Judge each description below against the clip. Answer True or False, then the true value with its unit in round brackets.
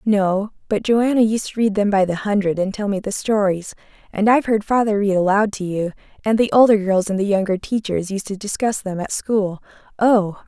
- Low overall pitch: False (205 Hz)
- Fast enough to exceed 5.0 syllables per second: True (5.3 syllables/s)